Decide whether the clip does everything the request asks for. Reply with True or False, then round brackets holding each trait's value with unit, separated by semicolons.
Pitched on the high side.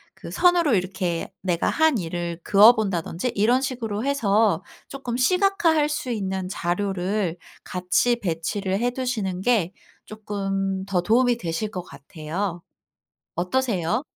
True (200 Hz)